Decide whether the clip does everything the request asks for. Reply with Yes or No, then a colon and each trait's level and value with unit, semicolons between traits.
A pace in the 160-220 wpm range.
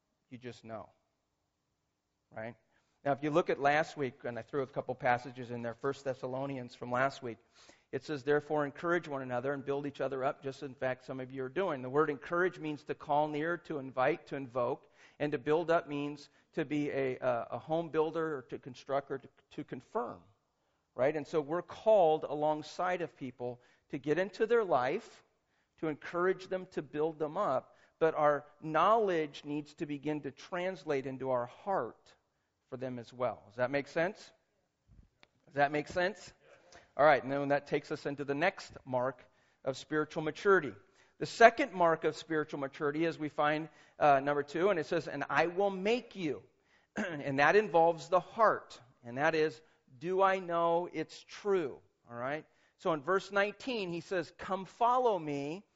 Yes: average, 185 wpm